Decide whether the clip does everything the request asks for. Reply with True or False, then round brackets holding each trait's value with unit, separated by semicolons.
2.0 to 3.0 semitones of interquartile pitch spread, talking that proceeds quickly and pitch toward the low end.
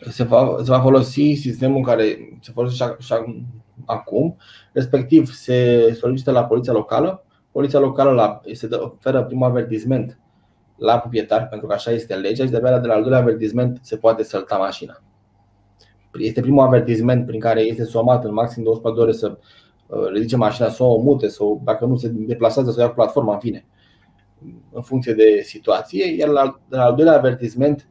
True (2.5 semitones; 175 wpm; 120 Hz)